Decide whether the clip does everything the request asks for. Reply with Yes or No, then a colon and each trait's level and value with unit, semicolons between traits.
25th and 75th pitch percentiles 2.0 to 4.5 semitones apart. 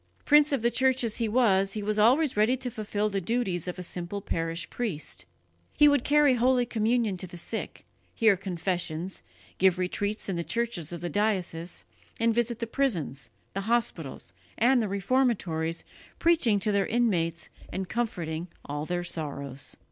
No: wide, 5.5 semitones